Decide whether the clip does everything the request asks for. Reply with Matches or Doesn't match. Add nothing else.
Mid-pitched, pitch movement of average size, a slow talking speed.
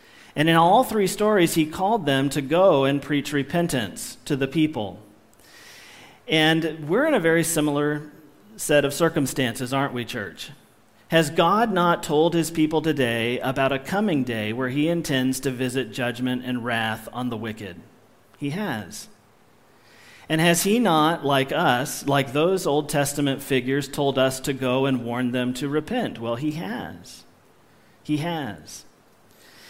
Doesn't match